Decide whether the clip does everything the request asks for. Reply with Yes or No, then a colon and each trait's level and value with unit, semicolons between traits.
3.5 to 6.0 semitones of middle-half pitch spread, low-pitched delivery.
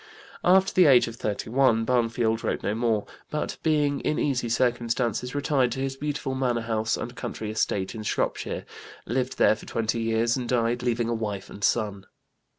No: average, 2.8 semitones; low, 120 Hz